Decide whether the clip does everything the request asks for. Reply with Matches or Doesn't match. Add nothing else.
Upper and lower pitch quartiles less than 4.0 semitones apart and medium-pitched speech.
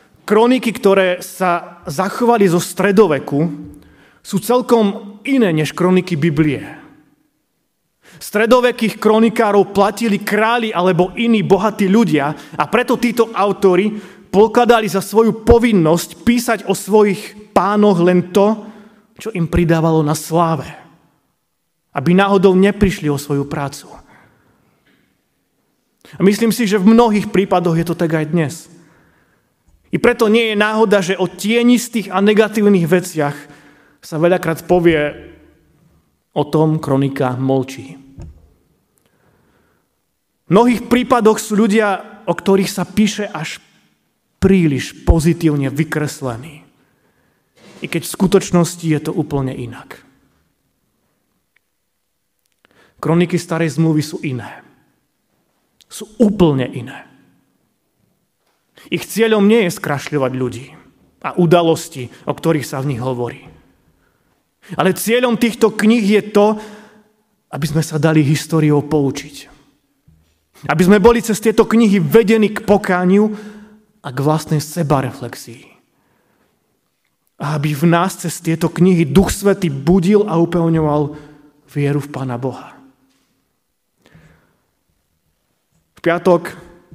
Doesn't match